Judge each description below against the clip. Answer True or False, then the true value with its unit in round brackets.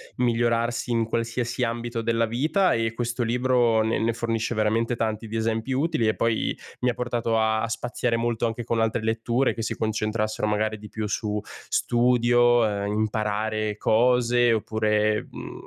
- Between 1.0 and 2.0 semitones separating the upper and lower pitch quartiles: True (1.6 semitones)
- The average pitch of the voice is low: True (115 Hz)